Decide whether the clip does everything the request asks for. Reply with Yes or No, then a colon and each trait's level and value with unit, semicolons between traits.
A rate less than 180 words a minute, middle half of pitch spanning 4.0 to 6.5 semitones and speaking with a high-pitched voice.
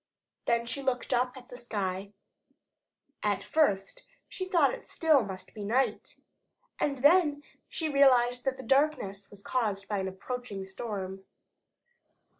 Yes: average, 140 wpm; wide, 5.6 semitones; high, 245 Hz